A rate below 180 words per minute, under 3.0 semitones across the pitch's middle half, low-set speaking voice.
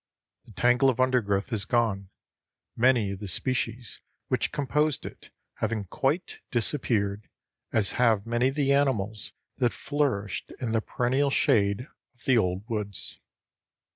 No: average, 140 wpm; average, 4.2 semitones; low, 115 Hz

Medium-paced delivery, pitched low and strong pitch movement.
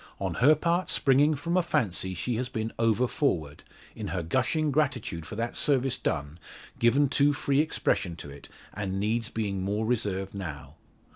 Yes: average, 170 wpm; low, 115 Hz; wide, 7.0 semitones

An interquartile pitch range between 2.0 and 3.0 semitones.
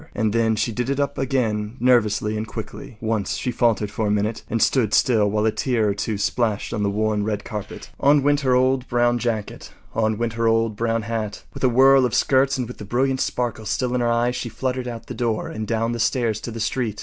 Yes: narrow, 2.6 semitones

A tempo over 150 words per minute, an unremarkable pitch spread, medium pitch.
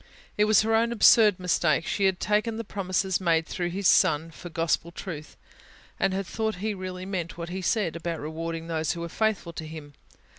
Yes: average, 195 wpm; average, 3.5 semitones; medium, 180 Hz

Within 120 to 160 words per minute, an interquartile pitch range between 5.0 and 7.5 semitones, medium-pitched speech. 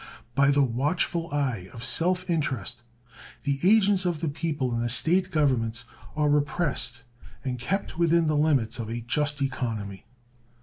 Yes: average, 150 wpm; wide, 5.5 semitones; medium, 145 Hz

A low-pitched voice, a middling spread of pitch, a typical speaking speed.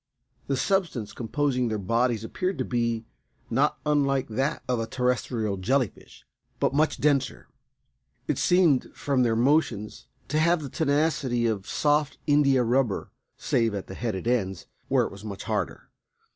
Yes: low, 125 Hz; average, 4.5 semitones; average, 150 wpm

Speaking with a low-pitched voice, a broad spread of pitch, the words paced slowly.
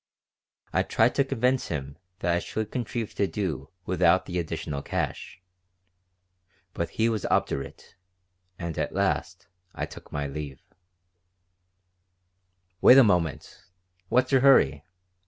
Yes: very low, 90 Hz; wide, 7.5 semitones; slow, 125 wpm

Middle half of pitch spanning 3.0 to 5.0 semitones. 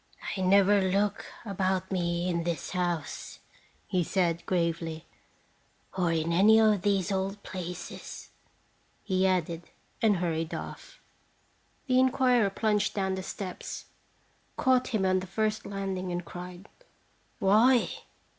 No: narrow, 2.6 semitones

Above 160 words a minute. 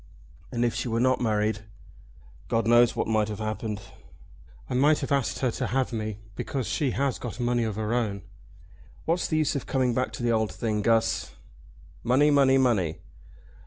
Yes: average, 185 wpm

